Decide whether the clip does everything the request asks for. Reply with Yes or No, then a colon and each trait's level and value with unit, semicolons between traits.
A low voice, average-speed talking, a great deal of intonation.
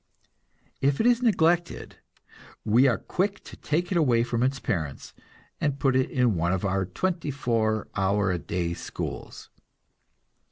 Yes: low, 125 Hz; average, 155 wpm; wide, 8.4 semitones